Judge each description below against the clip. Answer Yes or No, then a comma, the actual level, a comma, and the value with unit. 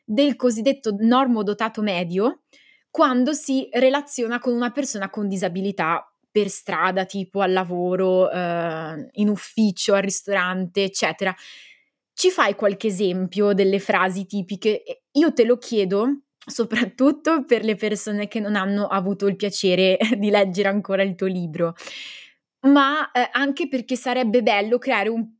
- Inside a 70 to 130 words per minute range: No, average, 140 wpm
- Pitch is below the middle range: No, high, 210 Hz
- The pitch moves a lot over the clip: No, average, 4.2 semitones